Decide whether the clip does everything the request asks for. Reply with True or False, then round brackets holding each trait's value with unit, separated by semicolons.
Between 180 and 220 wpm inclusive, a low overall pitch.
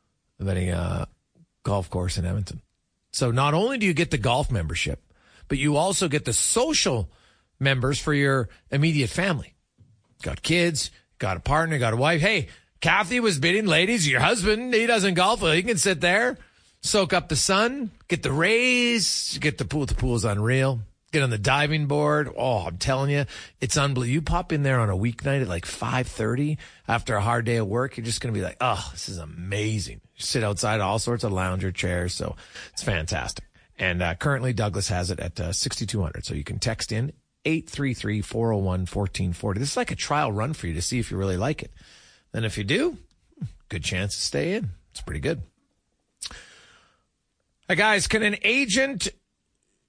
True (190 wpm; 125 Hz)